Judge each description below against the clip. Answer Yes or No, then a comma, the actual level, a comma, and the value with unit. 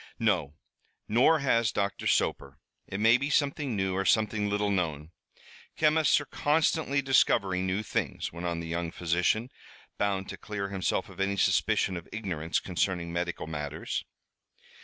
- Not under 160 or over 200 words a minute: No, average, 150 wpm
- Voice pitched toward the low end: Yes, low, 100 Hz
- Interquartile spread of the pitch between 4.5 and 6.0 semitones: Yes, average, 5.0 semitones